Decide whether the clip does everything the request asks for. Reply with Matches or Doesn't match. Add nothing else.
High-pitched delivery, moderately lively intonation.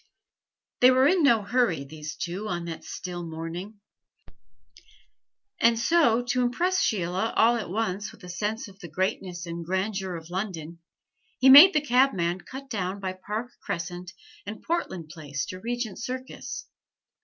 Doesn't match